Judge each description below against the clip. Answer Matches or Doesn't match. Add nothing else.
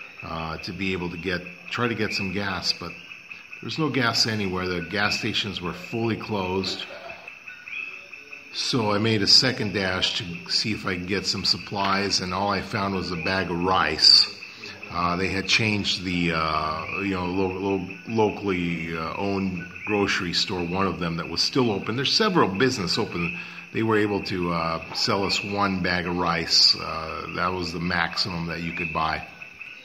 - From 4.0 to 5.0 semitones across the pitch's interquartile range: Doesn't match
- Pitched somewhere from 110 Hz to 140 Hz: Doesn't match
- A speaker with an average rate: Matches